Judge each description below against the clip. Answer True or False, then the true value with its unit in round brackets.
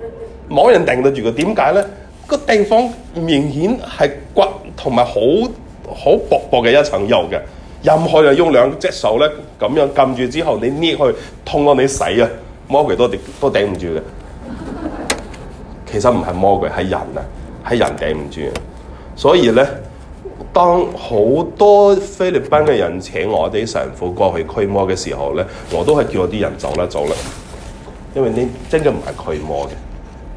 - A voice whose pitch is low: True (125 Hz)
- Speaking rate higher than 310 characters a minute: False (230 characters per minute)